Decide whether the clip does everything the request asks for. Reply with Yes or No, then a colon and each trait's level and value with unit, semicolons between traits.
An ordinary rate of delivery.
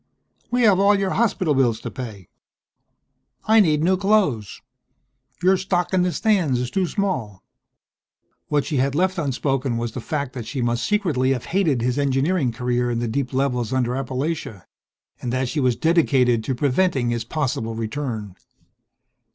Yes: average, 160 wpm